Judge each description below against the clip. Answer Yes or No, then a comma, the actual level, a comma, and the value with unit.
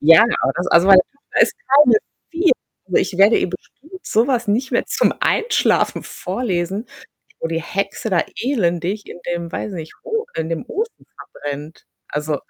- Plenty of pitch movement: Yes, wide, 7.0 semitones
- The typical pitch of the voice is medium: No, high, 195 Hz